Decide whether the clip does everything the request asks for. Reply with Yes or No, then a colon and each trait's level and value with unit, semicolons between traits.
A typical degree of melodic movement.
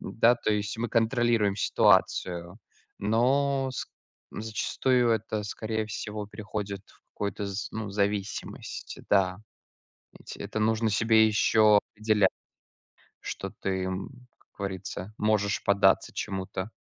No: narrow, 2.0 semitones